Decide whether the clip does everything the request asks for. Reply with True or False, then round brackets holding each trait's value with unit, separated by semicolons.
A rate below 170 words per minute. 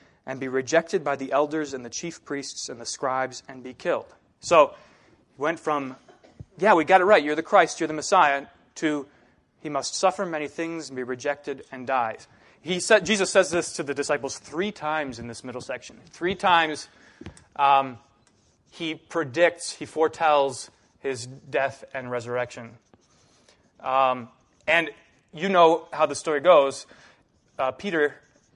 True (160 wpm)